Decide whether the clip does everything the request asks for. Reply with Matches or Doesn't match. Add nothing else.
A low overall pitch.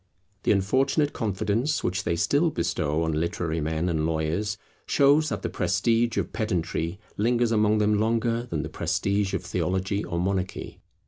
Matches